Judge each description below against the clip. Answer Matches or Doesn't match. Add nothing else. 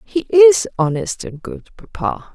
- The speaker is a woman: Matches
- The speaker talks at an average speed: Matches